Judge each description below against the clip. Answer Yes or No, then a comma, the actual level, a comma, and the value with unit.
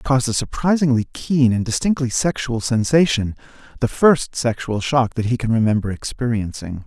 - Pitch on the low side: Yes, low, 120 Hz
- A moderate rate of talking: Yes, average, 155 wpm